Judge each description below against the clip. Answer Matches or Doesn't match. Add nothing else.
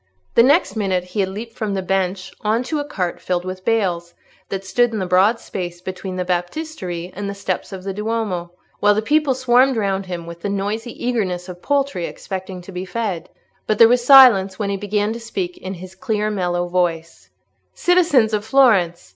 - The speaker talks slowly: Doesn't match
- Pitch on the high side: Matches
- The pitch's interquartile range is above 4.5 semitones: Doesn't match